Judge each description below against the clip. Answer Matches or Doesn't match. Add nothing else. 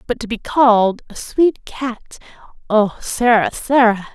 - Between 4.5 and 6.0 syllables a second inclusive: Doesn't match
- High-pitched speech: Matches